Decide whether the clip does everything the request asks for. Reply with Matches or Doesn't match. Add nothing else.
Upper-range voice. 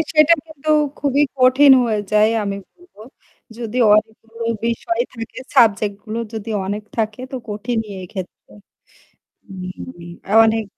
Matches